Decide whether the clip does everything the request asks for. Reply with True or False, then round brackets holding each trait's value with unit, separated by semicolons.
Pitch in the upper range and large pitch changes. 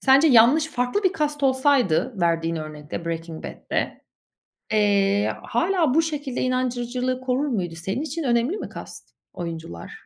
True (250 Hz; 8.3 semitones)